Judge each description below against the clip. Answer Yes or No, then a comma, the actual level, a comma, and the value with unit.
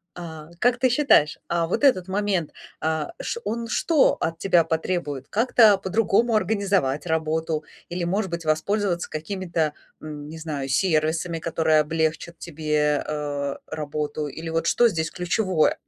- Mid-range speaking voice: Yes, medium, 165 Hz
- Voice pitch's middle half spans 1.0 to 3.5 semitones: No, average, 3.9 semitones